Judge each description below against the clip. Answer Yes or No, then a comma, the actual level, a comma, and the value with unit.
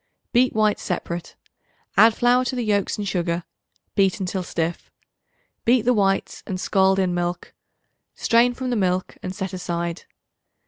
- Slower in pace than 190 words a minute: Yes, average, 150 wpm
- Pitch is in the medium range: No, high, 195 Hz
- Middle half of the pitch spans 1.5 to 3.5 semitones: No, average, 4.3 semitones